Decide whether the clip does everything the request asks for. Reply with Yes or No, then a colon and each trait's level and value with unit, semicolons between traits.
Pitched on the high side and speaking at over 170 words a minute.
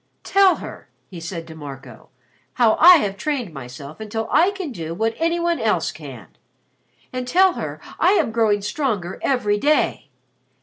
No: high, 225 Hz; average, 165 wpm